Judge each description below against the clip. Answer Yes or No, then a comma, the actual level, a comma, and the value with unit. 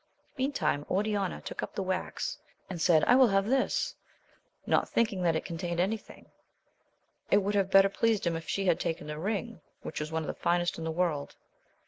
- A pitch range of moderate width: Yes, average, 3.9 semitones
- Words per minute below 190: No, average, 200 wpm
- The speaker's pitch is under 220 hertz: Yes, medium, 185 Hz